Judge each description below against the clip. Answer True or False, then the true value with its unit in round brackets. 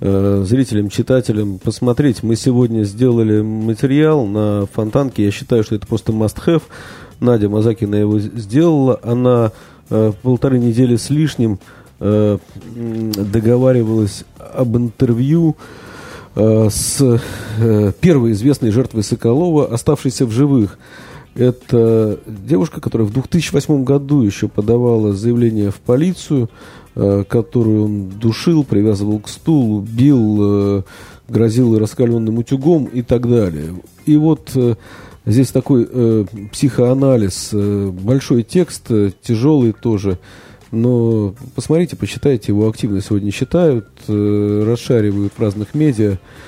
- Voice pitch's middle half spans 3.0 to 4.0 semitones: True (3.7 semitones)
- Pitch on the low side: True (115 Hz)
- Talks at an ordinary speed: False (105 wpm)